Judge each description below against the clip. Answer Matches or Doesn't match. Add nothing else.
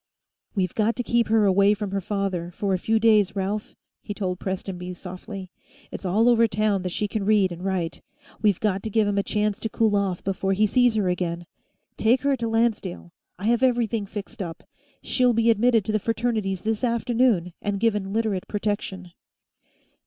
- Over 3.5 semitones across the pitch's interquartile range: Doesn't match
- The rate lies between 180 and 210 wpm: Matches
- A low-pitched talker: Doesn't match